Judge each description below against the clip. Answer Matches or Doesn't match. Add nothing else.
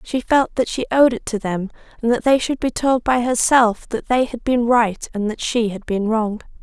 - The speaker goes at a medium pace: Doesn't match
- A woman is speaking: Matches